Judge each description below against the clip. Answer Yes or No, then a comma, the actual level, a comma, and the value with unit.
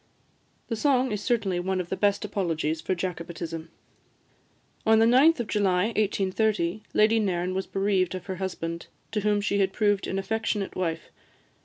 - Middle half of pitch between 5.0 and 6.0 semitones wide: No, average, 3.0 semitones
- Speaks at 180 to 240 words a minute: No, average, 165 wpm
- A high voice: Yes, high, 195 Hz